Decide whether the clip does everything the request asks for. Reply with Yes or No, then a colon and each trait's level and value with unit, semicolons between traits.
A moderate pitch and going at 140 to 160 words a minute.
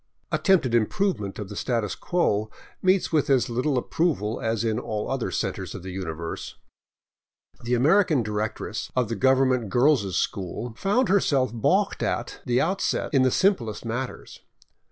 No: low, 125 Hz; average, 155 wpm